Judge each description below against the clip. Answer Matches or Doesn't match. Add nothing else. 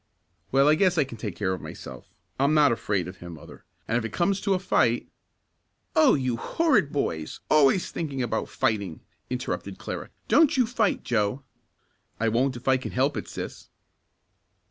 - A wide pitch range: Matches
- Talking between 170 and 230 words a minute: Matches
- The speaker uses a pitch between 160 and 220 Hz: Doesn't match